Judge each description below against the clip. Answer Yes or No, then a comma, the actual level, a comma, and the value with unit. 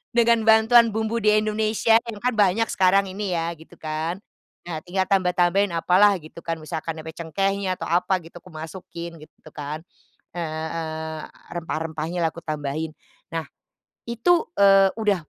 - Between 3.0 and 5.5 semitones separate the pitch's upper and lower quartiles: Yes, average, 4.5 semitones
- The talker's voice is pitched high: No, medium, 180 Hz